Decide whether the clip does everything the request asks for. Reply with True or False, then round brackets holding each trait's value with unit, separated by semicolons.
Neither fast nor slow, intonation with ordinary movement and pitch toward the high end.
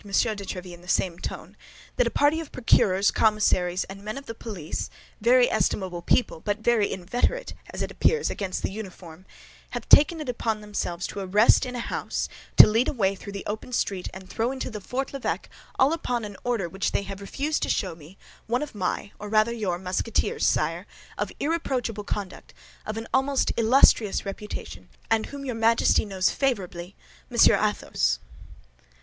True (170 wpm; 4.4 semitones; 210 Hz)